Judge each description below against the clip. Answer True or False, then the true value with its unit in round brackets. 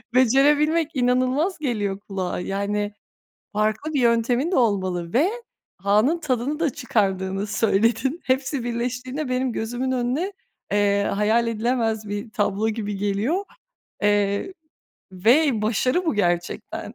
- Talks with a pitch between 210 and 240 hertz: True (230 Hz)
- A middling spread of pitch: True (4.2 semitones)